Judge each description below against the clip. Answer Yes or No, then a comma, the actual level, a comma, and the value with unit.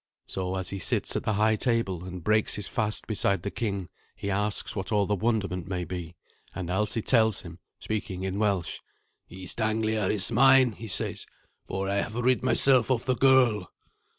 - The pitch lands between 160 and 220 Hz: No, low, 105 Hz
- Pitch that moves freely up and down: No, average, 3.0 semitones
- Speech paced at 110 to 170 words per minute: No, average, 185 wpm